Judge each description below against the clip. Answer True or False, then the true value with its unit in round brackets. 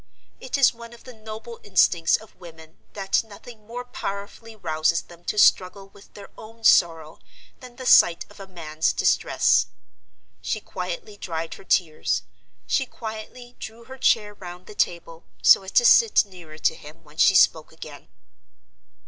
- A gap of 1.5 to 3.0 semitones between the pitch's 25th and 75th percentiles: False (5.2 semitones)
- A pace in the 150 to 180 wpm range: True (165 wpm)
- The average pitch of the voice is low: False (195 Hz)